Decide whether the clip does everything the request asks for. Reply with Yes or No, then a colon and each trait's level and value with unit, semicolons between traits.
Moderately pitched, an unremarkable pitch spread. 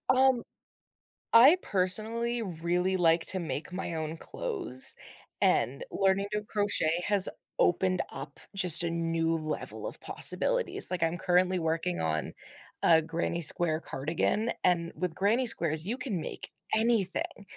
Yes: medium, 180 Hz; average, 4.2 semitones